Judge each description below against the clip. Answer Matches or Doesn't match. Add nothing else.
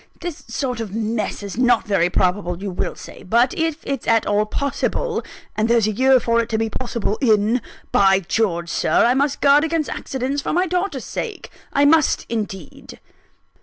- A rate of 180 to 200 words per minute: Matches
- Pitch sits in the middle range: Doesn't match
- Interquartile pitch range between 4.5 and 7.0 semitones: Matches